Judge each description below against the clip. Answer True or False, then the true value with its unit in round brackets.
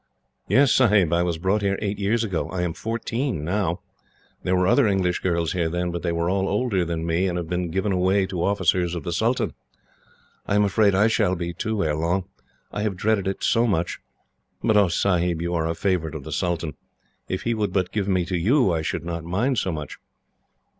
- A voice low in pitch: True (90 Hz)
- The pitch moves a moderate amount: True (3.2 semitones)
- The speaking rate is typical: False (220 wpm)